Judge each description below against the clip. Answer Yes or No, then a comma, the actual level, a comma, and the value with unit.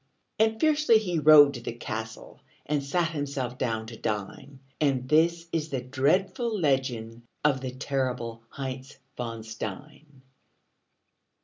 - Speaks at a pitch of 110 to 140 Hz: Yes, low, 135 Hz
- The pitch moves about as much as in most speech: Yes, average, 4.5 semitones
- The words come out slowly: Yes, slow, 130 wpm